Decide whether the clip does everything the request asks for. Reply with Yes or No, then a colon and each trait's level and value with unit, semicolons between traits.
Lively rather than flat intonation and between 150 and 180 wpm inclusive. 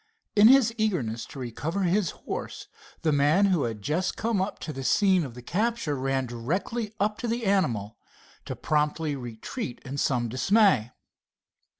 Yes: wide, 8.0 semitones; average, 165 wpm